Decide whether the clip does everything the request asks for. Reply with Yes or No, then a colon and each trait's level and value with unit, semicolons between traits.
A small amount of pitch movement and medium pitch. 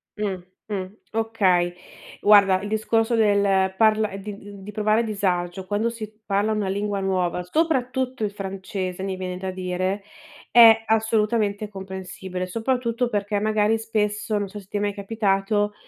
No: narrow, 2.3 semitones; high, 205 Hz